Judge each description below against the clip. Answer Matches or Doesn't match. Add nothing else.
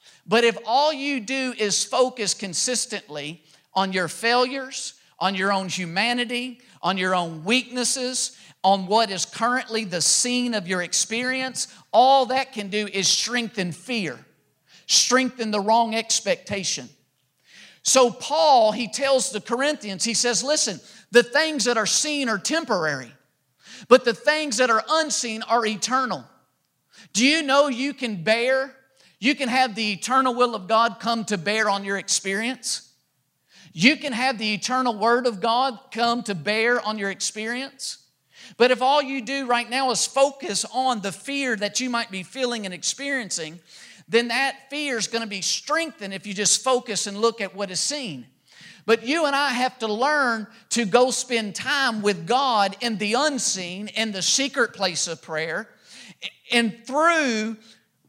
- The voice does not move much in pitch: Doesn't match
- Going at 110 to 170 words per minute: Matches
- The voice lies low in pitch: Doesn't match